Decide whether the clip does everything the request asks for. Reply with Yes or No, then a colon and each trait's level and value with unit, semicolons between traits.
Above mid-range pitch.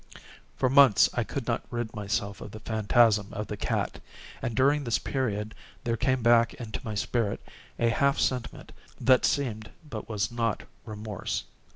No: low, 115 Hz